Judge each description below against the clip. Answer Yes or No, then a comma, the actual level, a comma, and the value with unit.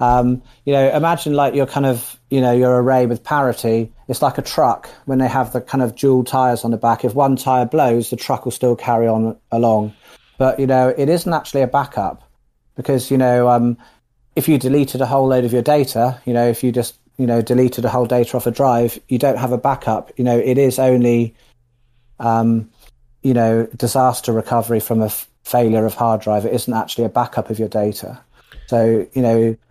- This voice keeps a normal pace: No, fast, 220 wpm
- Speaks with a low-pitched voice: Yes, low, 125 Hz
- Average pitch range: No, narrow, 2.0 semitones